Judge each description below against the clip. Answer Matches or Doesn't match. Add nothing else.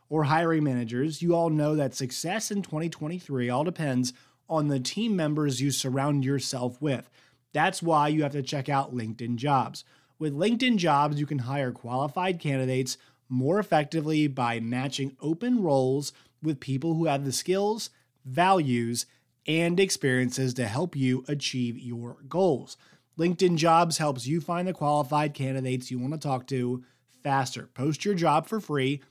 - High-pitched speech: Doesn't match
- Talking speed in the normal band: Matches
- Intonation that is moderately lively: Matches